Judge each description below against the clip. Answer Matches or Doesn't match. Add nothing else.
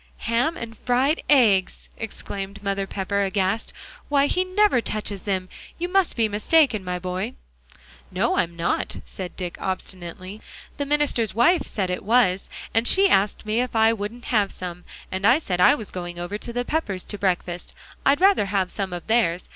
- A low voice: Doesn't match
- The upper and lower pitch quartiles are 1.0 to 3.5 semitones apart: Doesn't match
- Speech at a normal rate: Matches